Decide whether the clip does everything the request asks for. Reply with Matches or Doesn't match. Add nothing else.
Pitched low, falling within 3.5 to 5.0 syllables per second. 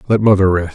Doesn't match